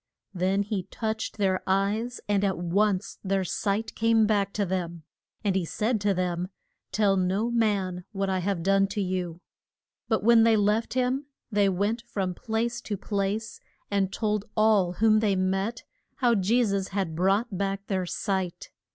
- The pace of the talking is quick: No, average, 170 wpm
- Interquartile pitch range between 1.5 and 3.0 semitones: Yes, narrow, 2.5 semitones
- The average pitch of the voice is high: Yes, high, 200 Hz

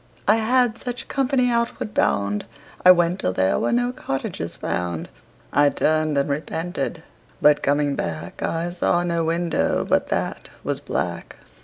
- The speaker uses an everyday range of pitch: No, wide, 7.7 semitones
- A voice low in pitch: No, medium, 165 Hz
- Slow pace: No, average, 150 wpm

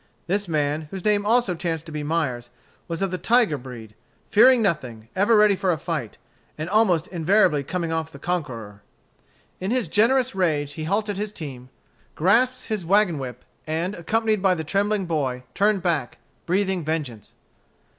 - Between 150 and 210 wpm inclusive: Yes, average, 165 wpm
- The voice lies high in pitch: No, medium, 175 Hz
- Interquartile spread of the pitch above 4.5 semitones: Yes, average, 5.3 semitones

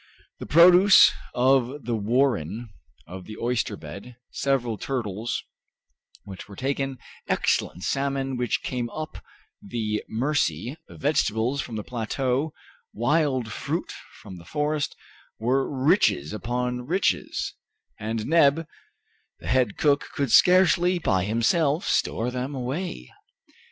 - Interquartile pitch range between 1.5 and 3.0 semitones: No, average, 4.3 semitones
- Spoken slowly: Yes, slow, 115 wpm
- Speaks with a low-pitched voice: Yes, low, 125 Hz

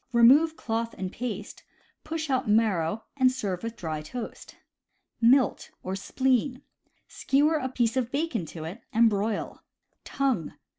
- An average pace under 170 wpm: Yes, average, 140 wpm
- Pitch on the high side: Yes, high, 230 Hz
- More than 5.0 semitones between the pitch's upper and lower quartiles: No, average, 4.4 semitones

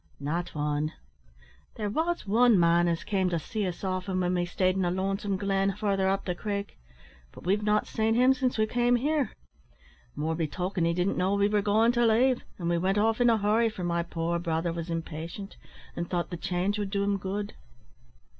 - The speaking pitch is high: Yes, high, 195 Hz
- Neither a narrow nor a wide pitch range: Yes, average, 3.5 semitones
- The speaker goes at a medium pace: No, fast, 210 wpm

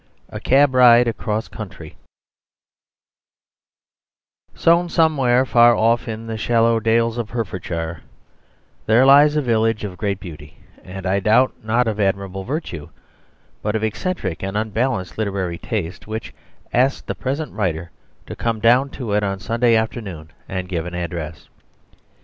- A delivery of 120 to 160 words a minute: Yes, average, 145 wpm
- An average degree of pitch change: Yes, average, 4.2 semitones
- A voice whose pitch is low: Yes, low, 110 Hz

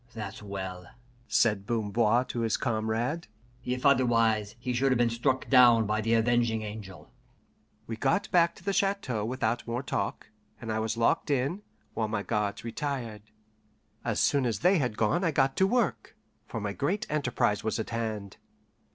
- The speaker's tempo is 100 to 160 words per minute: No, average, 170 wpm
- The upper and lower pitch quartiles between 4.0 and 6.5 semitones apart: No, average, 3.5 semitones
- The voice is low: Yes, low, 115 Hz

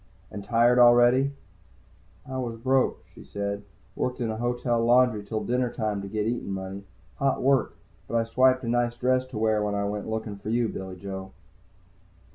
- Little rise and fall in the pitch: No, average, 3.1 semitones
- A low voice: Yes, low, 115 Hz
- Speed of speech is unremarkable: Yes, average, 185 wpm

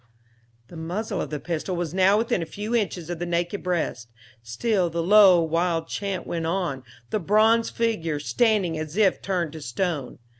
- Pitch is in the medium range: Yes, medium, 175 Hz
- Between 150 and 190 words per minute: Yes, average, 180 wpm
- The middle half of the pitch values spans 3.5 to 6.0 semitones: Yes, average, 3.8 semitones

